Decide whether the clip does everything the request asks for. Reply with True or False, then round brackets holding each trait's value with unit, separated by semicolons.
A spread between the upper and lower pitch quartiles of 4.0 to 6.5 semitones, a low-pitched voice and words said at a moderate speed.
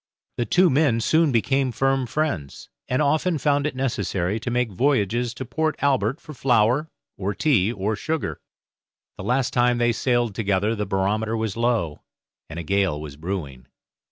True (5.3 semitones; 120 Hz; 165 wpm)